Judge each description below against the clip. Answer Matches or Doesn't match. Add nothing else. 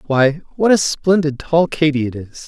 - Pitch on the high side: Doesn't match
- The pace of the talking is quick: Doesn't match